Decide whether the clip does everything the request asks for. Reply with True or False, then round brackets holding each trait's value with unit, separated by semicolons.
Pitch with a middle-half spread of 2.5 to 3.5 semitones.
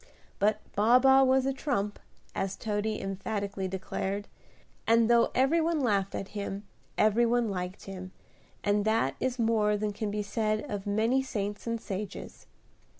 True (2.8 semitones)